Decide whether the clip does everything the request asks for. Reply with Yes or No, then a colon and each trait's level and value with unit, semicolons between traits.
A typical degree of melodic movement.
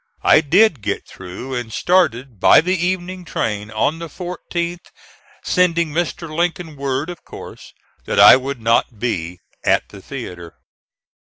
No: wide, 7.3 semitones